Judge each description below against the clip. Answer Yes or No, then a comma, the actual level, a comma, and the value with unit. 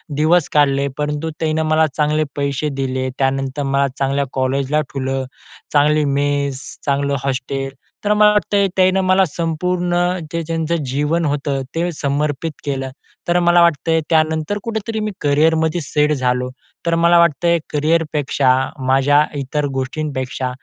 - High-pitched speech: No, medium, 150 Hz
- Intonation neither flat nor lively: Yes, average, 3.3 semitones